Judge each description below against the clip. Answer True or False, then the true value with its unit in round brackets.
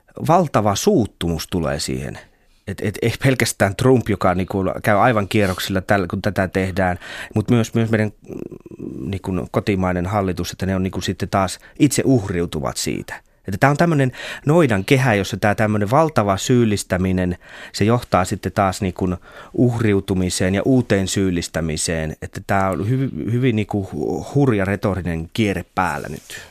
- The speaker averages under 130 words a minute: False (145 wpm)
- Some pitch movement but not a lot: True (3.5 semitones)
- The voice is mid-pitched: False (100 Hz)